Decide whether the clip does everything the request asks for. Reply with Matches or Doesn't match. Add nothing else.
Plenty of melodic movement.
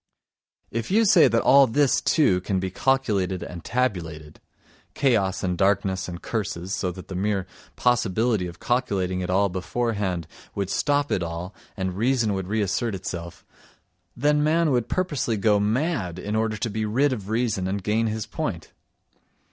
Doesn't match